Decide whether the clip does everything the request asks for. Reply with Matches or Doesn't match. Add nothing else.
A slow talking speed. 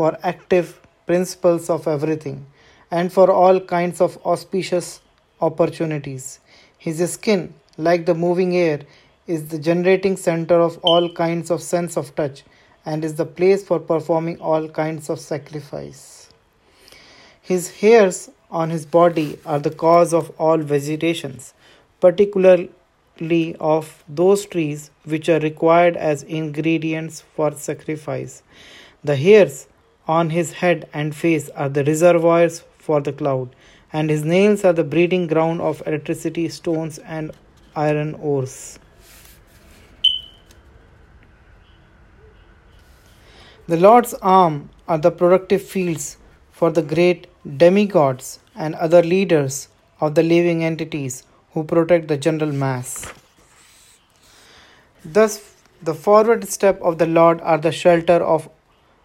Matches